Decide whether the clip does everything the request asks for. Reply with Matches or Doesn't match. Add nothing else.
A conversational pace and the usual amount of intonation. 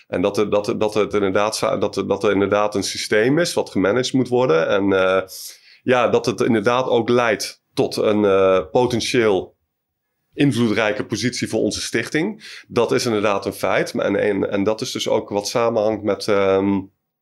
Matches